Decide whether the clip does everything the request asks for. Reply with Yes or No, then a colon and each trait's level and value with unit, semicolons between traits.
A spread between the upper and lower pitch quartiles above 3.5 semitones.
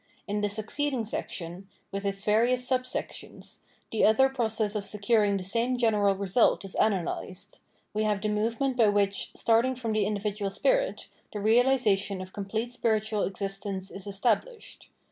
No: average, 2.9 semitones